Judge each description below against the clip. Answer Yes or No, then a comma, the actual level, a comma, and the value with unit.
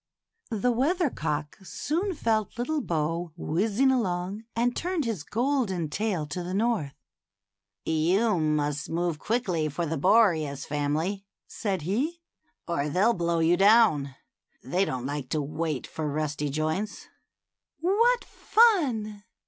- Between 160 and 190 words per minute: No, slow, 135 wpm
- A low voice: No, medium, 185 Hz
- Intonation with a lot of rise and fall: Yes, wide, 7.2 semitones